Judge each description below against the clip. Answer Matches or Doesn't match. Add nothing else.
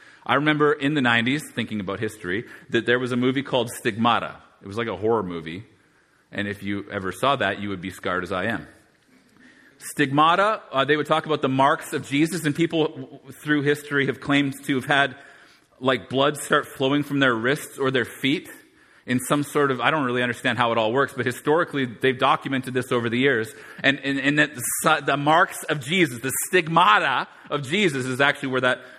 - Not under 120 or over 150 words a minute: Doesn't match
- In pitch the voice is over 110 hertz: Matches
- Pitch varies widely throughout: Doesn't match